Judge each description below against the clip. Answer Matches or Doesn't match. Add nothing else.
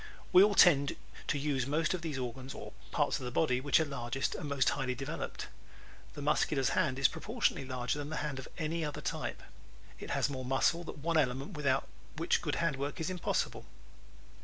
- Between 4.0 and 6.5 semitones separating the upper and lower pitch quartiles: Doesn't match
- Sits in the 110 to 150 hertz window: Matches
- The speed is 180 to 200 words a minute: Matches